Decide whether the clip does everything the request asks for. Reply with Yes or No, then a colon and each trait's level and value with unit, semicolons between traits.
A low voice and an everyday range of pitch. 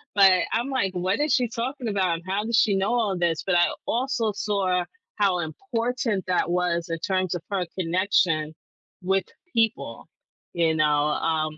No: high, 190 Hz; average, 4.6 semitones